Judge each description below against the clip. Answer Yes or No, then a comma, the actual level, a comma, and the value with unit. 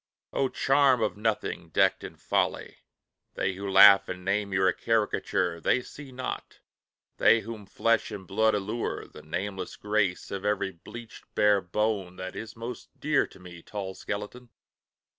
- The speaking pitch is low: Yes, low, 105 Hz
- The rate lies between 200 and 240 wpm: No, average, 160 wpm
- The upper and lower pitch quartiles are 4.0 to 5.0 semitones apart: No, average, 3.2 semitones